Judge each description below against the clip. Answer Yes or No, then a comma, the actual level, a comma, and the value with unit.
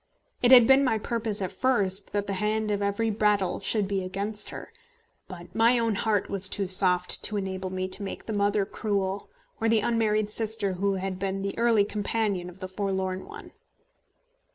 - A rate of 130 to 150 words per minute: No, average, 190 wpm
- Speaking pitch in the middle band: No, high, 200 Hz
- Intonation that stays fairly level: Yes, narrow, 2.3 semitones